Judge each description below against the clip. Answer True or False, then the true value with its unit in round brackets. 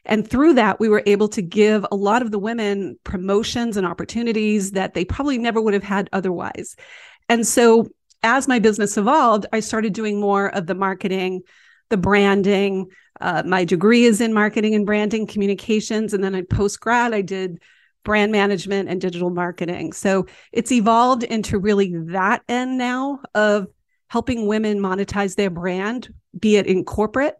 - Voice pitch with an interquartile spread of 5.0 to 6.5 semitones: False (2.9 semitones)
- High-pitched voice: True (210 Hz)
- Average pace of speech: True (170 wpm)